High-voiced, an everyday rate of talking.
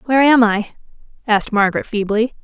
Yes: high, 225 Hz; average, 150 wpm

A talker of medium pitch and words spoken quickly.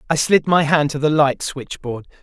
Yes: medium, 150 Hz; fast, 215 wpm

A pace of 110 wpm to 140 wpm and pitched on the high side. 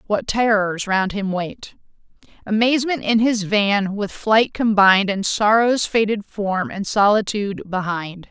Yes: slow, 135 wpm; high, 205 Hz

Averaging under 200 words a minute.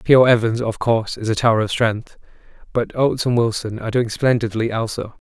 No: fast, 205 wpm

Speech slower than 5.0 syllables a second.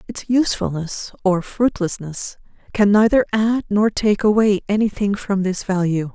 Yes: 4.5 syllables/s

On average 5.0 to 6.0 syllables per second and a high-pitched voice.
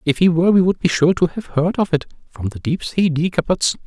No: 5.7 syllables/s; medium, 165 Hz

